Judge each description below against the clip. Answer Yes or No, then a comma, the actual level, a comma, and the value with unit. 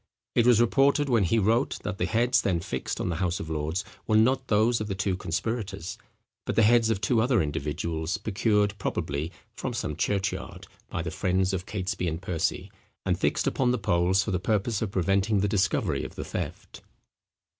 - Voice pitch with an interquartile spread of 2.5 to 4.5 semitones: Yes, average, 4.0 semitones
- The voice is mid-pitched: No, low, 100 Hz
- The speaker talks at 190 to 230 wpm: Yes, average, 200 wpm